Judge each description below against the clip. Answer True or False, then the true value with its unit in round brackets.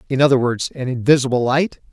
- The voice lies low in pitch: True (130 Hz)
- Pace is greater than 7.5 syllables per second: False (6.3 syllables/s)